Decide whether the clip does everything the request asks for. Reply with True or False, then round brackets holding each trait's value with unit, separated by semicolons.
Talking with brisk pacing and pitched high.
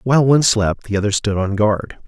False (230 wpm; 110 Hz)